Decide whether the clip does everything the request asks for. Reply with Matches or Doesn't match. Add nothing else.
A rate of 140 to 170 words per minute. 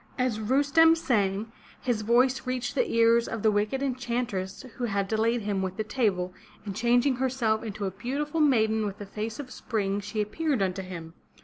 Doesn't match